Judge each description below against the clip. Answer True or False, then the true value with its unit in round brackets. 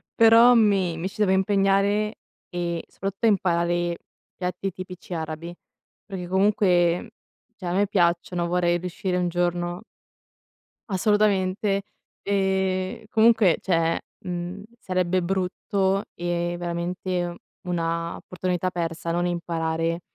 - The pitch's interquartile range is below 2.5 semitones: True (2.1 semitones)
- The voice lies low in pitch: False (180 Hz)